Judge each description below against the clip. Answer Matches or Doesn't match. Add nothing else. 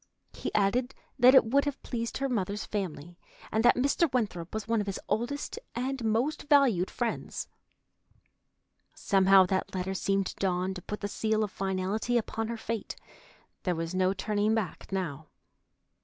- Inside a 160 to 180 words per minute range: Matches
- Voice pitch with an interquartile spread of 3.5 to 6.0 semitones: Matches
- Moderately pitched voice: Doesn't match